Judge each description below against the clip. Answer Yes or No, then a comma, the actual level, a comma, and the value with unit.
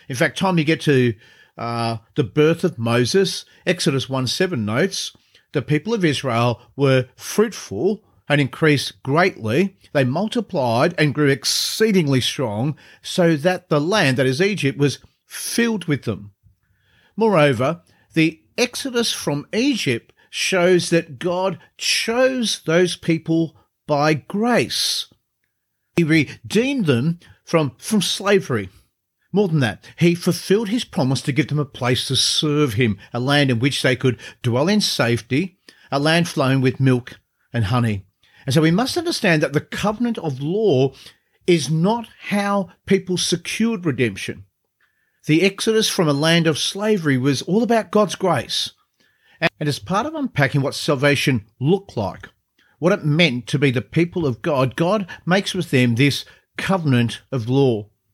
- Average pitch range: No, wide, 6.5 semitones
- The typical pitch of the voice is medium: Yes, medium, 150 Hz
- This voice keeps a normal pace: Yes, average, 150 wpm